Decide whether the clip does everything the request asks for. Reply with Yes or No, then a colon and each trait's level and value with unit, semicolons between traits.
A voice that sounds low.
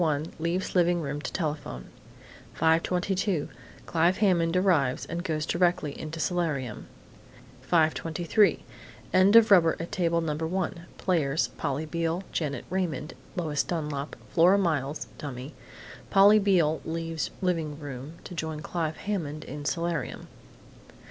No: medium, 165 Hz